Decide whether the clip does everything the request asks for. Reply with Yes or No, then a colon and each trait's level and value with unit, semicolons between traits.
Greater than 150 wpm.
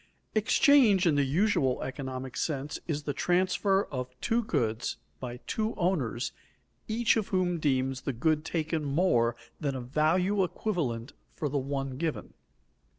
No: average, 145 wpm